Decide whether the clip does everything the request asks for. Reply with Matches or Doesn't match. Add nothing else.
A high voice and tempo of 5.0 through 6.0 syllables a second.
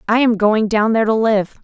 Matches